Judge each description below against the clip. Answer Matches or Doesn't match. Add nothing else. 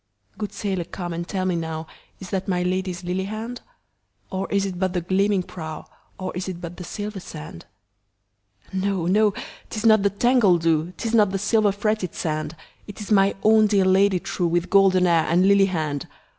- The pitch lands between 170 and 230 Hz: Matches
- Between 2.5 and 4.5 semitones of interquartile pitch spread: Matches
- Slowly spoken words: Doesn't match